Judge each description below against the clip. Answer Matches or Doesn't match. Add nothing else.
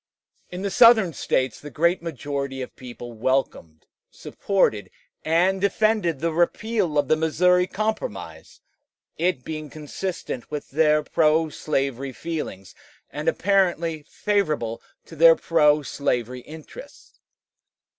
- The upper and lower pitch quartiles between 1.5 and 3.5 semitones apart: Doesn't match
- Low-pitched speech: Doesn't match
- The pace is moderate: Doesn't match